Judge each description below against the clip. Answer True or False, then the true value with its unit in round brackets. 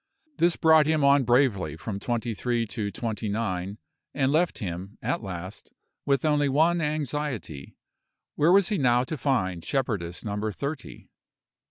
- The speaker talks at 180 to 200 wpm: False (150 wpm)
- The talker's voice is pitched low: True (125 Hz)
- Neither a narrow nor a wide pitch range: False (6.5 semitones)